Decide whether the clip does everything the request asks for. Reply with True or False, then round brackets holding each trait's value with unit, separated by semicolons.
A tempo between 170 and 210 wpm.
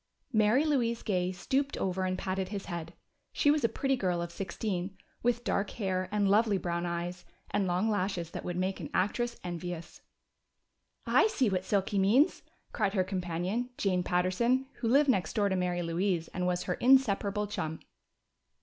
True (175 wpm)